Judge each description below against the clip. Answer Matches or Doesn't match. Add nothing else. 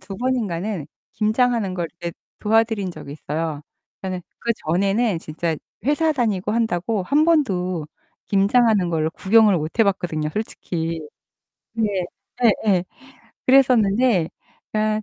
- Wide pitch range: Doesn't match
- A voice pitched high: Matches